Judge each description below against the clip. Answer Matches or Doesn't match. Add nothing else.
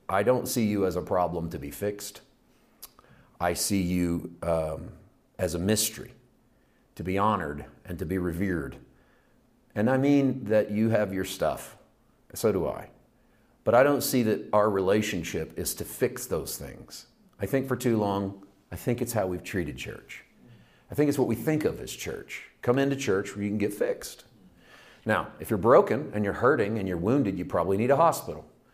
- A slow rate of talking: Doesn't match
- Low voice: Matches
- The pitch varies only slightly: Doesn't match